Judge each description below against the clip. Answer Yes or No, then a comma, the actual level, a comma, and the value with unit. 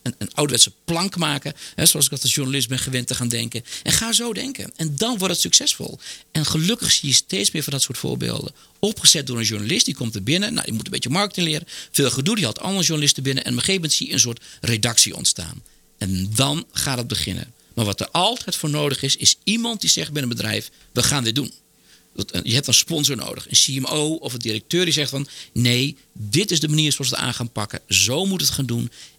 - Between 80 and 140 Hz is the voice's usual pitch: Yes, low, 135 Hz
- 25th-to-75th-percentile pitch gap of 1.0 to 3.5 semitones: No, average, 5.2 semitones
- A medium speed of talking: No, fast, 245 wpm